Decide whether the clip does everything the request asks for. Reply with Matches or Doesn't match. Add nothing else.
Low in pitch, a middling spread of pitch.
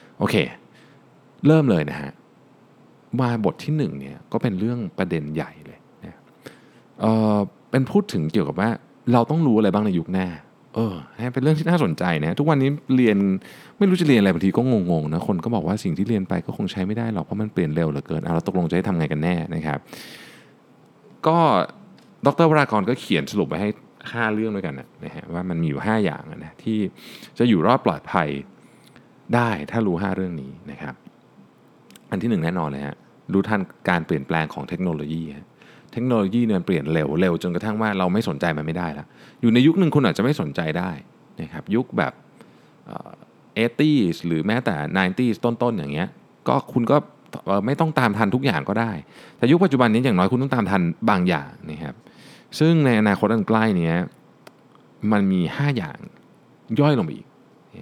Doesn't match